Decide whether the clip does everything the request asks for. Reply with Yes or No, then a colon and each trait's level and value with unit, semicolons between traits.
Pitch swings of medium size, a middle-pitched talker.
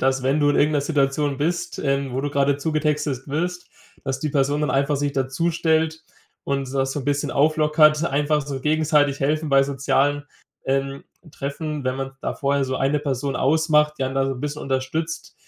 No: narrow, 1.9 semitones; medium, 145 Hz